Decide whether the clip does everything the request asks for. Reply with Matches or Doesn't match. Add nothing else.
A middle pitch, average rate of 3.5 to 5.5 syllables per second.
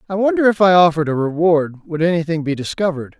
Doesn't match